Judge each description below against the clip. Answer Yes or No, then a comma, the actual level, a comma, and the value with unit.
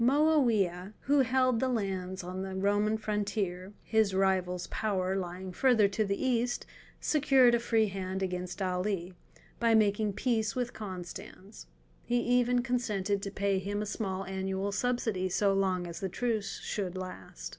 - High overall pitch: Yes, high, 200 Hz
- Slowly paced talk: No, average, 145 wpm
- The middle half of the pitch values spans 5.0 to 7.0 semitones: No, average, 3.8 semitones